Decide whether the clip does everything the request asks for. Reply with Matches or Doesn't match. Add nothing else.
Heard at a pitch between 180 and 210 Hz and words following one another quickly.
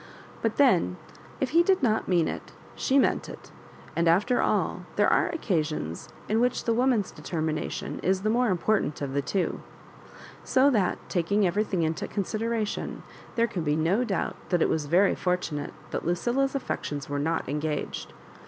Doesn't match